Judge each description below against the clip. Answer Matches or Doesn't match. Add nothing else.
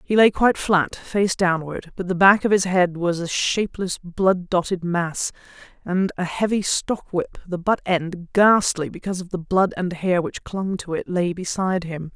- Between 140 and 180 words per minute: Doesn't match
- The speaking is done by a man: Doesn't match